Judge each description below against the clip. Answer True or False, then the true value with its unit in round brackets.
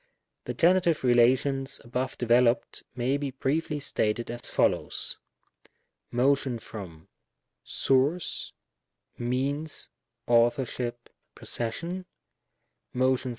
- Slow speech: True (70 wpm)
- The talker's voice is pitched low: True (125 Hz)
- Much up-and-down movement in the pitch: False (3.0 semitones)